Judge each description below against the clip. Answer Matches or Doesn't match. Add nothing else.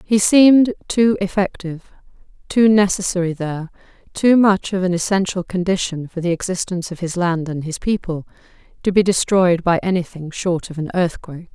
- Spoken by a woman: Matches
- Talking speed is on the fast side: Doesn't match